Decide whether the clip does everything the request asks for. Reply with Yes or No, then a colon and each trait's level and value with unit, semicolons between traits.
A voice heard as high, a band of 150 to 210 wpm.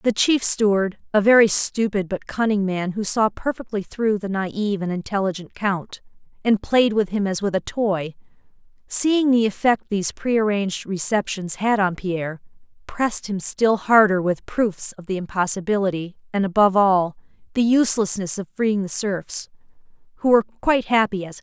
Yes: high, 205 Hz; average, 170 wpm